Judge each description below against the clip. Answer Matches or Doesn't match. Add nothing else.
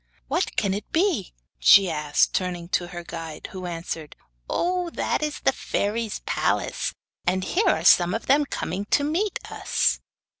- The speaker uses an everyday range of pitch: Doesn't match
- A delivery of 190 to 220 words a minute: Doesn't match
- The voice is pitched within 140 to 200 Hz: Matches